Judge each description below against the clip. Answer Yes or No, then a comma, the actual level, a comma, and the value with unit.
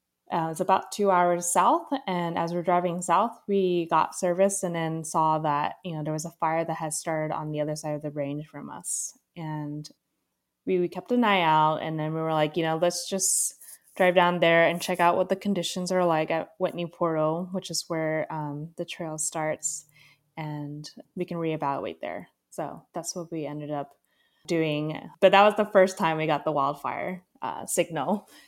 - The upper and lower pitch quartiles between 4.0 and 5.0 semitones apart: No, average, 2.8 semitones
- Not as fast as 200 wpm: No, fast, 205 wpm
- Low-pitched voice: No, medium, 165 Hz